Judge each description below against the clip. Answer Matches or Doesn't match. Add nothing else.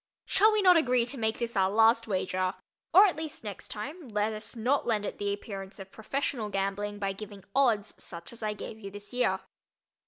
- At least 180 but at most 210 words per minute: Matches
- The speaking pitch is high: Matches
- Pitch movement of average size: Matches